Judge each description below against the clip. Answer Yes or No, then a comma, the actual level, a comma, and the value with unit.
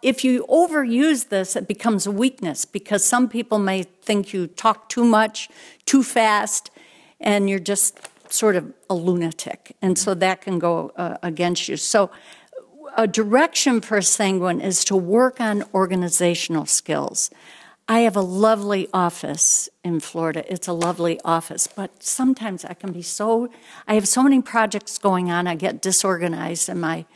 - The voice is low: No, high, 200 Hz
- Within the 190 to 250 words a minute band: No, average, 165 wpm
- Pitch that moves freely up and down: No, average, 4.2 semitones